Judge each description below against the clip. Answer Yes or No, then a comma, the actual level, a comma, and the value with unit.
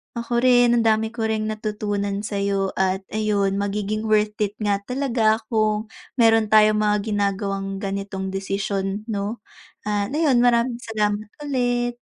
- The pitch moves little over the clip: Yes, narrow, 2.1 semitones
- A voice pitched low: No, high, 215 Hz